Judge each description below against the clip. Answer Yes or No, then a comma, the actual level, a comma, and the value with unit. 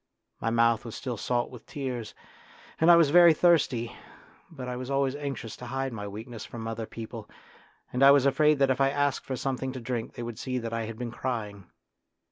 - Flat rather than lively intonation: No, average, 3.1 semitones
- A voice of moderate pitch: No, low, 125 Hz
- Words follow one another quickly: Yes, fast, 215 wpm